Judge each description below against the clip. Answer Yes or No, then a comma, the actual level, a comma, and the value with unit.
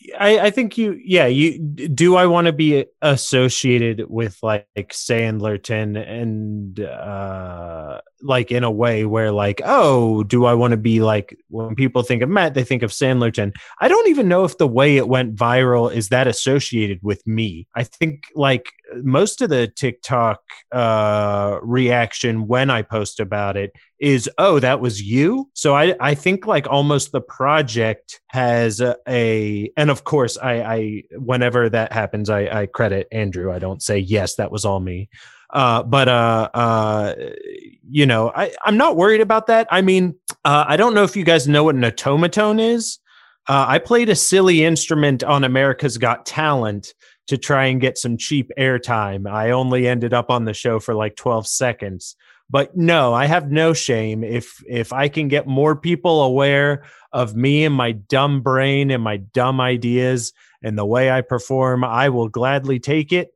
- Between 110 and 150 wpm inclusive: No, average, 180 wpm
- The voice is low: Yes, low, 125 Hz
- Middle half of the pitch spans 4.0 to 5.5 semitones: Yes, average, 4.6 semitones